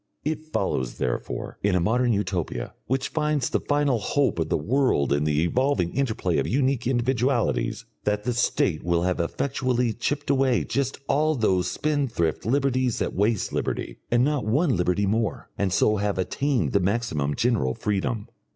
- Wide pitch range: Yes, wide, 6.6 semitones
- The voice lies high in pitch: No, low, 115 Hz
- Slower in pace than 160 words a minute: No, average, 165 wpm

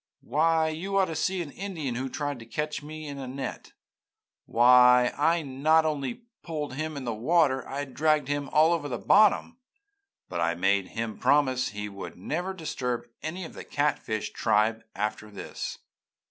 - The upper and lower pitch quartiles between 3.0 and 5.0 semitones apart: Yes, average, 4.5 semitones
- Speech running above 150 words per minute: Yes, average, 175 wpm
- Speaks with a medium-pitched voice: Yes, medium, 145 Hz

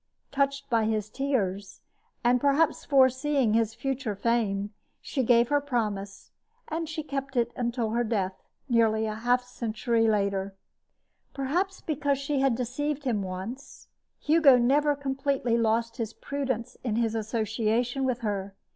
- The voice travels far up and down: No, average, 4.0 semitones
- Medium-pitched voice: No, high, 240 Hz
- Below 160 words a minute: Yes, average, 140 wpm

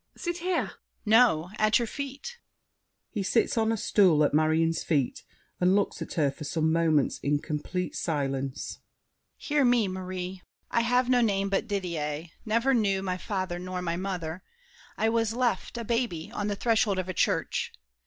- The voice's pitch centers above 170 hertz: Yes, high, 190 Hz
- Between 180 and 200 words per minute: No, average, 170 wpm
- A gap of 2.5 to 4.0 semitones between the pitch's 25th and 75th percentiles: No, wide, 5.6 semitones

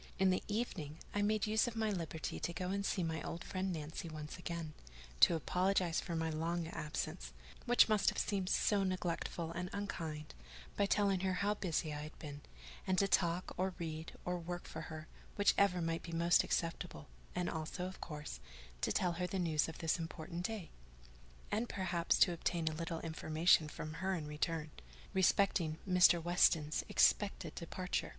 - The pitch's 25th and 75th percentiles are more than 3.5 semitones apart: No, average, 2.8 semitones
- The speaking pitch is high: No, medium, 170 Hz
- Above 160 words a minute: Yes, average, 180 wpm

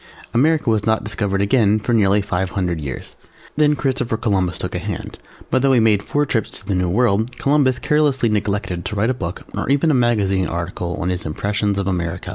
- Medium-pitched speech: No, low, 105 Hz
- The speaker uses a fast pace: Yes, fast, 210 wpm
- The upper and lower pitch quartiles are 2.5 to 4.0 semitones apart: No, average, 4.7 semitones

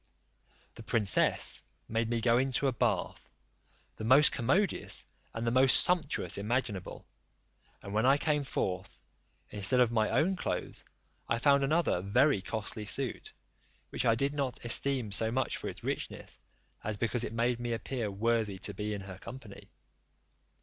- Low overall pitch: Yes, low, 115 Hz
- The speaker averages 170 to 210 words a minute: No, average, 155 wpm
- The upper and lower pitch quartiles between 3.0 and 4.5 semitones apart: Yes, average, 3.9 semitones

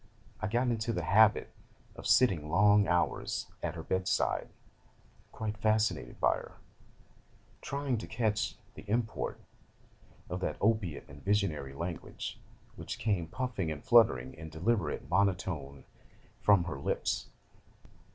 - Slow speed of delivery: Yes, slow, 130 wpm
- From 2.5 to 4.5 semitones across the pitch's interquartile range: No, average, 5.1 semitones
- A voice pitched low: Yes, low, 100 Hz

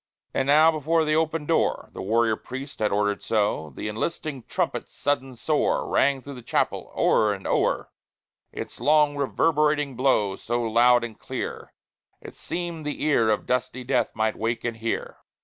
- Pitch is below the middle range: Yes, low, 130 Hz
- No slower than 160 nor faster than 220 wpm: Yes, average, 165 wpm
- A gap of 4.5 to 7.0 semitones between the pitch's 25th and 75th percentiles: Yes, average, 4.9 semitones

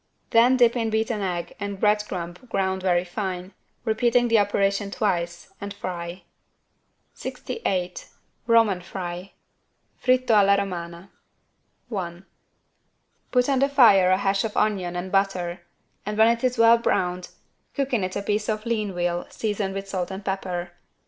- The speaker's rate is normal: Yes, average, 150 wpm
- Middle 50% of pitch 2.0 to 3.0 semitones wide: No, average, 3.4 semitones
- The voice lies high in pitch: Yes, high, 195 Hz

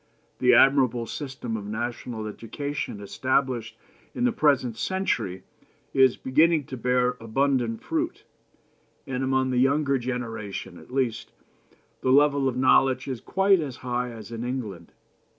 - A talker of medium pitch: No, low, 130 Hz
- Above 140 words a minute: No, slow, 135 wpm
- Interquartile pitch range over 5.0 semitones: No, average, 3.1 semitones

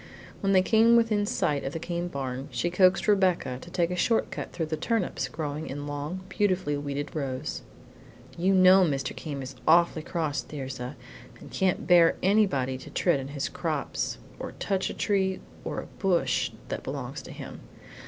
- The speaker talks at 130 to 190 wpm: Yes, average, 180 wpm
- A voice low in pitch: No, medium, 170 Hz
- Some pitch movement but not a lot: Yes, average, 4.9 semitones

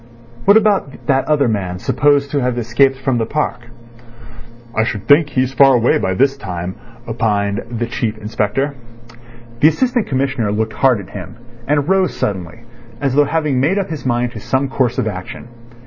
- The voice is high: No, low, 130 Hz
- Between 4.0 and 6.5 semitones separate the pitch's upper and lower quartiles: Yes, average, 4.5 semitones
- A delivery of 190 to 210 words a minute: No, average, 180 wpm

